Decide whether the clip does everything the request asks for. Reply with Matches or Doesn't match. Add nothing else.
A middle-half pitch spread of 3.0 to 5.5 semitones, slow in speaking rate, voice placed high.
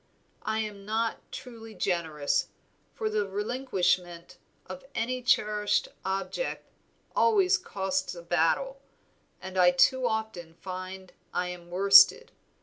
Matches